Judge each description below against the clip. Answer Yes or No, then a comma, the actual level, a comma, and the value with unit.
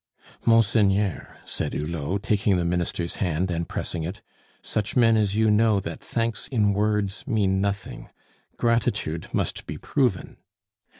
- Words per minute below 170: Yes, slow, 135 wpm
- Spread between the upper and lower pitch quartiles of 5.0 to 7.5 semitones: No, average, 3.7 semitones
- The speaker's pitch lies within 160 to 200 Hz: No, low, 100 Hz